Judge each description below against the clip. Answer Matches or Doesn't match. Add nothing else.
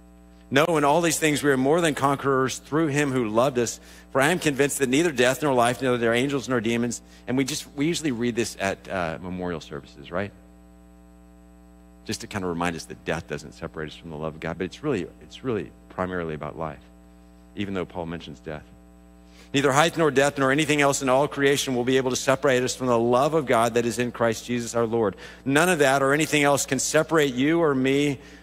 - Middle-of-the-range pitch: Doesn't match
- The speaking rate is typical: Doesn't match